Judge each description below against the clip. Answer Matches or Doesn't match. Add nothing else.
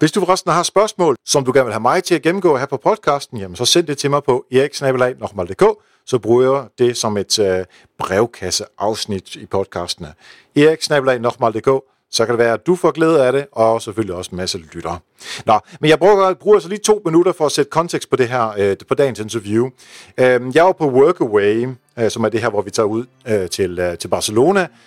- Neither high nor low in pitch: Doesn't match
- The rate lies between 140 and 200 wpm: Doesn't match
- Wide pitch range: Matches